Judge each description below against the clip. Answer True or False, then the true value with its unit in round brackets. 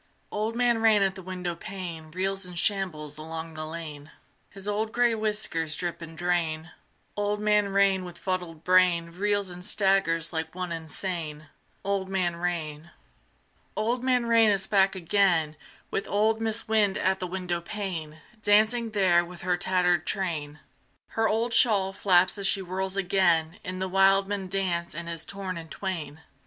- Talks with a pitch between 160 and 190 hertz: True (185 Hz)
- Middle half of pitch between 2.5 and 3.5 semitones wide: True (3.1 semitones)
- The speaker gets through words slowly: False (160 wpm)